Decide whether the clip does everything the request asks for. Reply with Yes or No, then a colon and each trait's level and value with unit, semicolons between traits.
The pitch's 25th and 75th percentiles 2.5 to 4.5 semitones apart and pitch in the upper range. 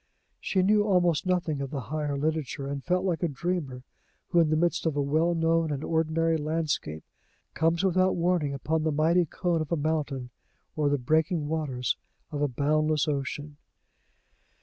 No: average, 2.8 semitones; medium, 155 Hz